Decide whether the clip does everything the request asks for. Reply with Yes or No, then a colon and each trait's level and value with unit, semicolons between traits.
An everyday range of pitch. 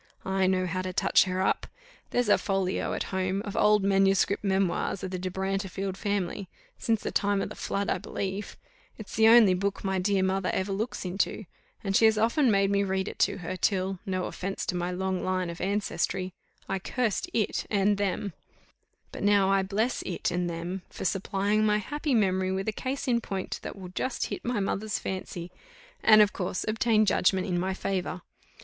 No: narrow, 1.8 semitones